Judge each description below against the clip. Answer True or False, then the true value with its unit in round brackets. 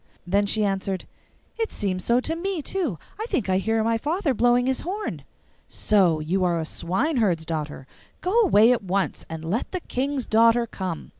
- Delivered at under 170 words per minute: False (180 wpm)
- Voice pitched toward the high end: True (220 Hz)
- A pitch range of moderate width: False (6.7 semitones)